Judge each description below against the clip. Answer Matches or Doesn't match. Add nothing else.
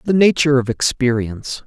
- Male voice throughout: Matches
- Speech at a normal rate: Matches